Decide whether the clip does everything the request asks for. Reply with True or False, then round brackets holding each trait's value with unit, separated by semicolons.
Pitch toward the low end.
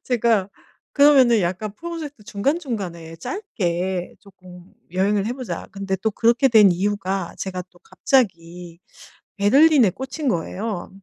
False (205 Hz)